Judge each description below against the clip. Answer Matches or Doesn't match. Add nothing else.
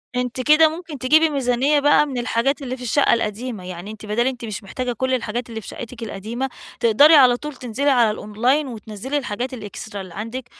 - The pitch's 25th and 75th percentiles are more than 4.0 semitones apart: Doesn't match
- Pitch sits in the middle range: Doesn't match